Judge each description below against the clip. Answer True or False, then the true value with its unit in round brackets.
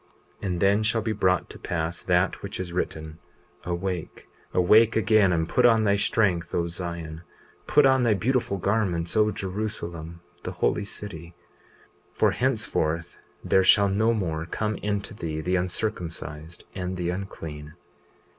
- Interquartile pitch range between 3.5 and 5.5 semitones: True (3.9 semitones)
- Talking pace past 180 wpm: False (150 wpm)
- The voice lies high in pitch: False (95 Hz)